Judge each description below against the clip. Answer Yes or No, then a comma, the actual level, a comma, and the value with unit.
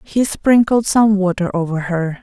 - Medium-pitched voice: No, high, 195 Hz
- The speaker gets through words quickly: No, average, 160 wpm